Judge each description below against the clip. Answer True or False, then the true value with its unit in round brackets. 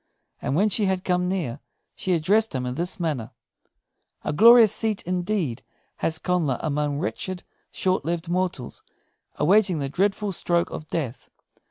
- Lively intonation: False (4.3 semitones)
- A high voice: False (180 Hz)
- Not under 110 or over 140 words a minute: False (150 wpm)